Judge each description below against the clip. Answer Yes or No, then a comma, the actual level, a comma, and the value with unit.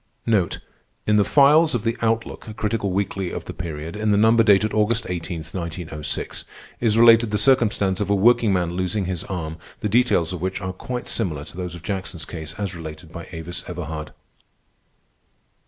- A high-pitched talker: No, very low, 95 Hz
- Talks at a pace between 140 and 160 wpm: No, average, 175 wpm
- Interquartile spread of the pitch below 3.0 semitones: No, average, 4.2 semitones